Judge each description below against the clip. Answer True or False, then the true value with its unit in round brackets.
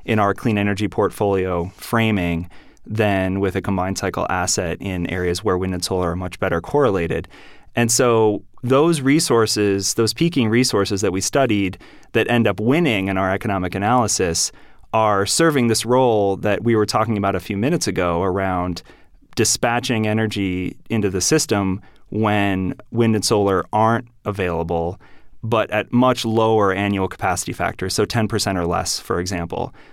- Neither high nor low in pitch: False (100 Hz)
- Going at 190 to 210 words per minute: False (155 wpm)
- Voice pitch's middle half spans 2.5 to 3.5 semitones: True (3.1 semitones)